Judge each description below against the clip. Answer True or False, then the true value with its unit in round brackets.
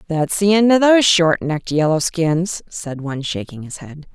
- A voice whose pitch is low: False (170 Hz)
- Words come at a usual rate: True (190 wpm)